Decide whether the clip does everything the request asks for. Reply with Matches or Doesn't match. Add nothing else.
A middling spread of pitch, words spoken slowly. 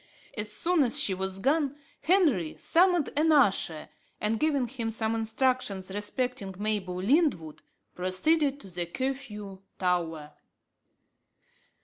Doesn't match